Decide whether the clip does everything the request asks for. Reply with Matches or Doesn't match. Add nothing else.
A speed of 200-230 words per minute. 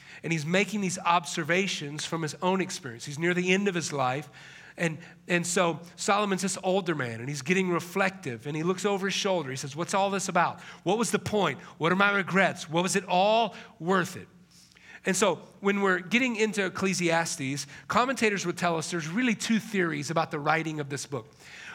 Matches